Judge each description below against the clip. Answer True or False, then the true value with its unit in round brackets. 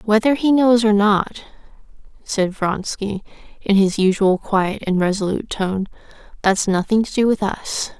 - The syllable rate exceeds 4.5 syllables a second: False (4.4 syllables/s)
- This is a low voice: False (205 Hz)